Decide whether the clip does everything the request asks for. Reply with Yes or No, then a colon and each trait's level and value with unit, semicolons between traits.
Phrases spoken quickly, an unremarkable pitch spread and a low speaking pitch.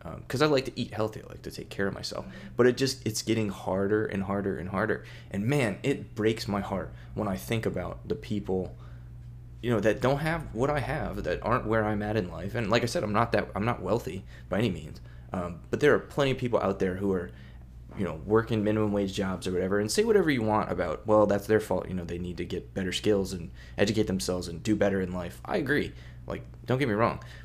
Yes: fast, 245 wpm; average, 4.2 semitones; low, 105 Hz